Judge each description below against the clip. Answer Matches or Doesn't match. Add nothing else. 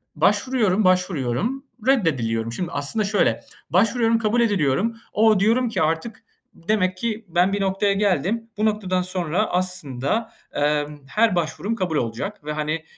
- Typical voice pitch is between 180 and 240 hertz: Matches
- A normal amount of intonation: Doesn't match